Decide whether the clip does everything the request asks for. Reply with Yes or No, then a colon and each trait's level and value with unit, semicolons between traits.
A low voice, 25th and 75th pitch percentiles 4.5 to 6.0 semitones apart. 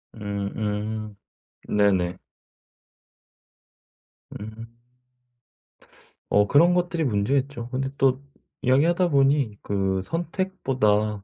Yes: low, 115 Hz; wide, 5.4 semitones